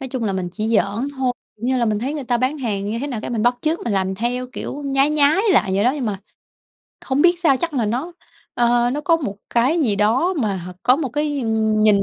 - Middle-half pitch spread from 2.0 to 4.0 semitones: No, average, 4.8 semitones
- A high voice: Yes, high, 245 Hz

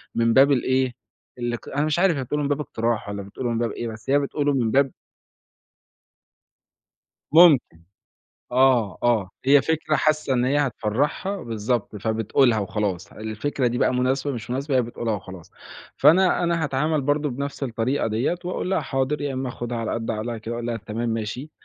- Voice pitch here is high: No, low, 125 Hz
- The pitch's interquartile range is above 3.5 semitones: Yes, average, 4.1 semitones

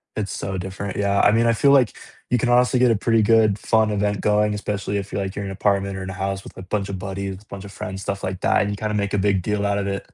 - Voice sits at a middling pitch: No, low, 100 Hz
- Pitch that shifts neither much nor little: No, narrow, 1.5 semitones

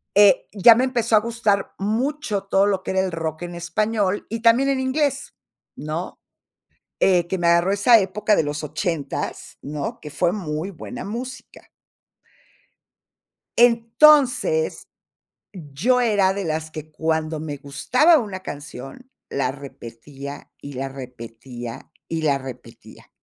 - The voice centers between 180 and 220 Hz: Yes, medium, 185 Hz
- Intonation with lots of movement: Yes, wide, 7.2 semitones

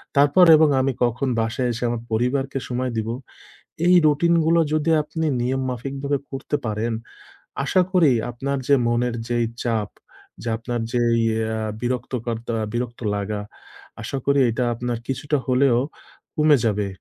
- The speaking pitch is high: No, low, 125 Hz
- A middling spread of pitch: Yes, average, 3.2 semitones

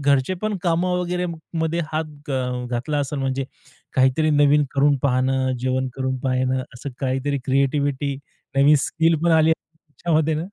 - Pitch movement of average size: Yes, average, 3.3 semitones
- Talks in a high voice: No, medium, 145 Hz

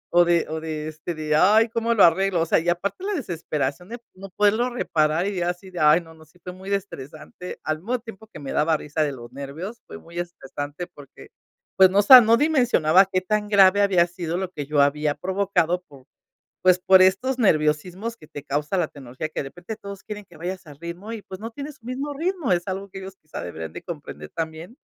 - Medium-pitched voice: Yes, medium, 180 Hz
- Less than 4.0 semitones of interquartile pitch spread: No, average, 4.6 semitones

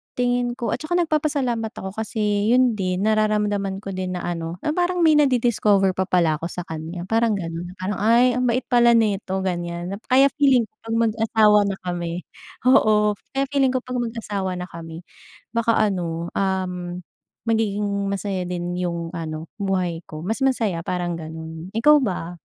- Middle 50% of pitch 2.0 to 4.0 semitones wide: No, average, 4.9 semitones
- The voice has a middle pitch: No, high, 200 Hz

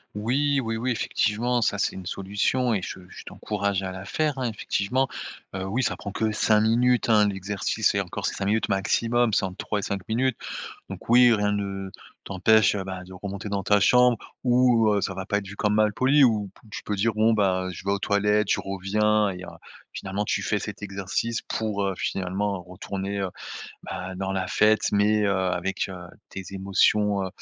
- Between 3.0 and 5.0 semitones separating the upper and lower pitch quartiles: No, narrow, 2.4 semitones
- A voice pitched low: Yes, low, 105 Hz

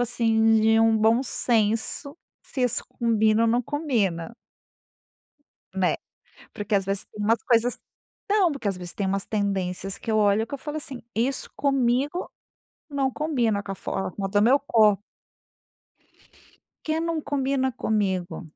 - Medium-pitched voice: No, high, 225 Hz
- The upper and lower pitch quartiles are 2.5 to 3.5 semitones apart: No, average, 4.5 semitones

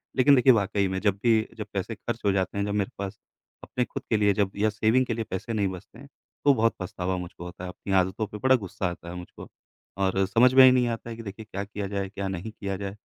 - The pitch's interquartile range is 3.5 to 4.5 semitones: No, average, 3.0 semitones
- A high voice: No, low, 100 Hz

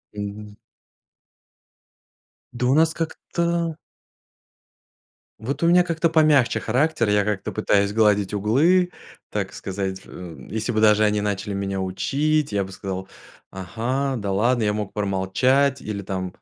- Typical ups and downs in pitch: No, wide, 5.9 semitones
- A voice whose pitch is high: No, low, 105 Hz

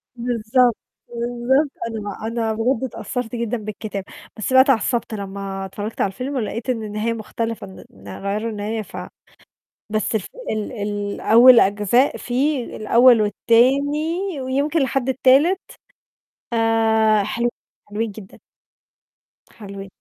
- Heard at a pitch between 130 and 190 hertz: No, high, 230 Hz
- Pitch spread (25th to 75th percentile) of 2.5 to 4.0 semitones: Yes, average, 3.3 semitones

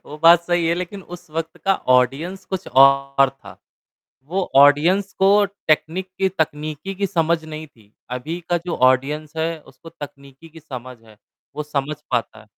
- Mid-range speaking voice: Yes, medium, 155 Hz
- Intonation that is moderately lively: Yes, average, 4.2 semitones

